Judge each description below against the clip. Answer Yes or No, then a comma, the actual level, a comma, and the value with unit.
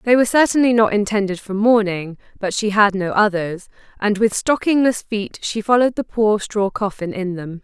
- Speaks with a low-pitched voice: No, high, 210 Hz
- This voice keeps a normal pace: Yes, average, 190 wpm